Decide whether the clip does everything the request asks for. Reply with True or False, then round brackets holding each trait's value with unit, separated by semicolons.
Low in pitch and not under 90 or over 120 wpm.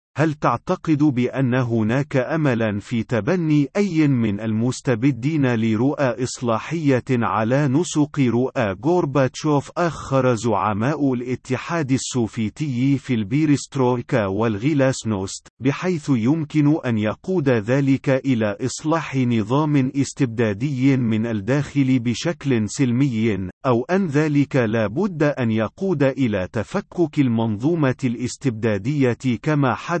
True (130 Hz; 100 wpm)